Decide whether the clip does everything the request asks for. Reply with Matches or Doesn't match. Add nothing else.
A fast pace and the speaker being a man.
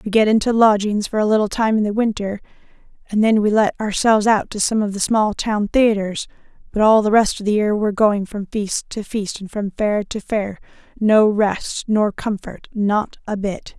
Doesn't match